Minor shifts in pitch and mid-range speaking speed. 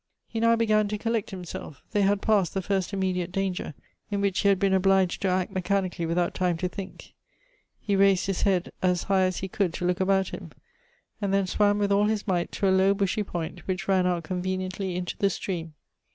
No: narrow, 1.7 semitones; fast, 215 wpm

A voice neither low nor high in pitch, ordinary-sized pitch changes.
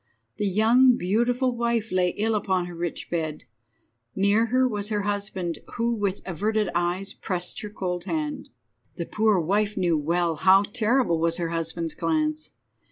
No: high, 195 Hz; average, 4.1 semitones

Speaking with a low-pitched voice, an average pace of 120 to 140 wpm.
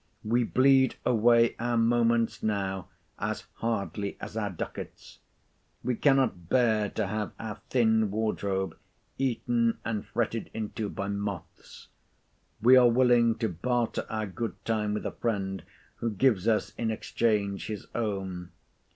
Yes: low, 110 Hz; slow, 135 wpm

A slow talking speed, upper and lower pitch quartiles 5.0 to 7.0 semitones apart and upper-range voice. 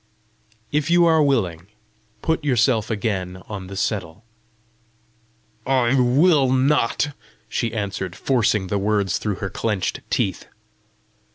No: slow, 115 wpm; wide, 5.5 semitones; low, 110 Hz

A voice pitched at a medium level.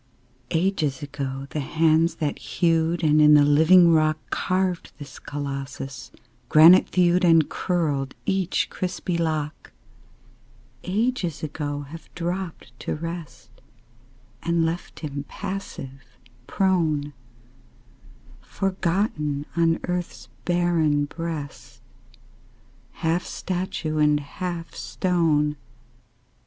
Yes: medium, 160 Hz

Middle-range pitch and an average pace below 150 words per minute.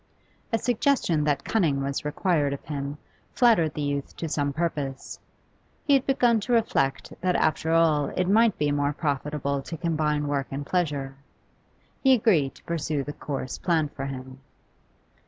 No: medium, 150 Hz; average, 160 wpm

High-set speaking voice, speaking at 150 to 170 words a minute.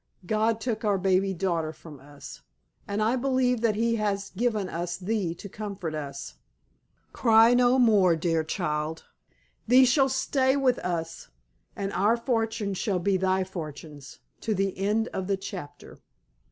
Yes: high, 200 Hz; average, 155 wpm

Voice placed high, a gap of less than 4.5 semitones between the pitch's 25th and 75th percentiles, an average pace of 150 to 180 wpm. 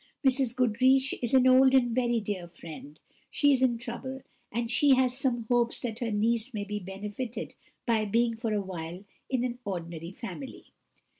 Yes: high, 235 Hz; average, 3.7 semitones; average, 175 wpm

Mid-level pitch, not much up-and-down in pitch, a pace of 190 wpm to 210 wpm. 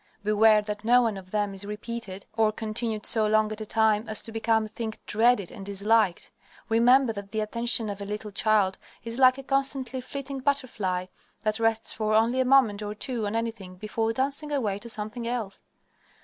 No: high, 220 Hz; narrow, 2.2 semitones; average, 195 wpm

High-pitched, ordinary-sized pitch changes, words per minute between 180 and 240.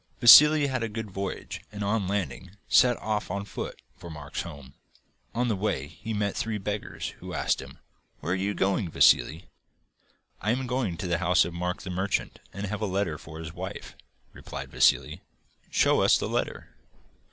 No: low, 100 Hz; average, 3.7 semitones; average, 185 wpm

